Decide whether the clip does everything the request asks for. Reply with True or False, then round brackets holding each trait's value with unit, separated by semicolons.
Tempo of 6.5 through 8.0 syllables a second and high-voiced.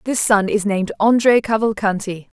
False (5.1 syllables/s; 210 Hz)